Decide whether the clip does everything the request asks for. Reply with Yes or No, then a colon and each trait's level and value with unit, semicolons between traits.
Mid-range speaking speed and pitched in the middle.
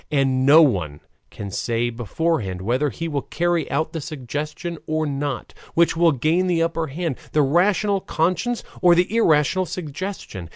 Yes: average, 160 wpm; medium, 155 Hz